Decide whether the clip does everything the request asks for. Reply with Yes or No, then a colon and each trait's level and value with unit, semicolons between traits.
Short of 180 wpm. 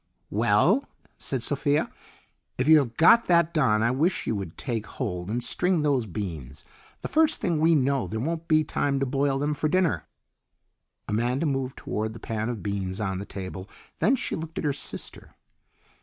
No: average, 185 wpm